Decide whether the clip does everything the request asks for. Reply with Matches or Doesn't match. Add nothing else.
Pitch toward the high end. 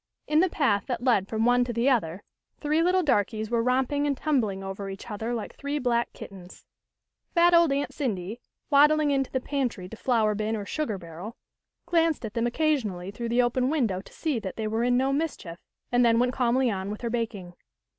Matches